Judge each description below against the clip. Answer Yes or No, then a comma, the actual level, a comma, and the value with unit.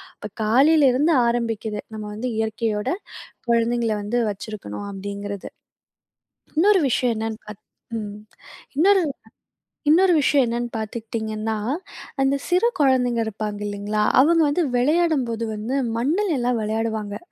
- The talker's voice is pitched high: Yes, high, 230 Hz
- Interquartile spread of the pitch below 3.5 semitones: No, average, 4.2 semitones